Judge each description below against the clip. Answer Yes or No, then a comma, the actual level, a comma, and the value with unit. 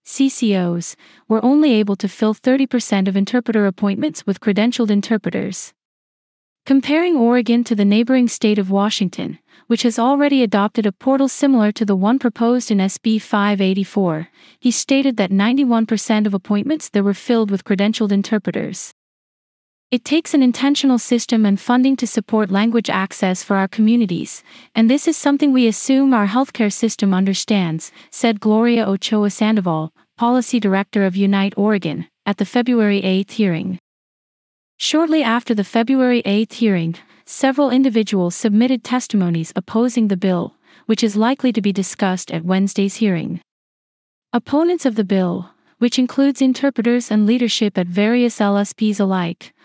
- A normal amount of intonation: Yes, average, 3.7 semitones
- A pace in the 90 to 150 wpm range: Yes, average, 145 wpm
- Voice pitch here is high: Yes, high, 220 Hz